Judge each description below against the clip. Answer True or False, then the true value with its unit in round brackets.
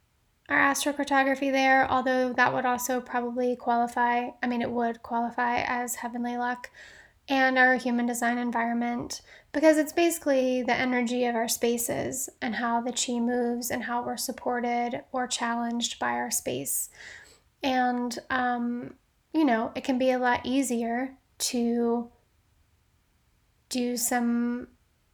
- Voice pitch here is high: True (245 Hz)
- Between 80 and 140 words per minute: True (135 wpm)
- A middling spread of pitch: False (1.4 semitones)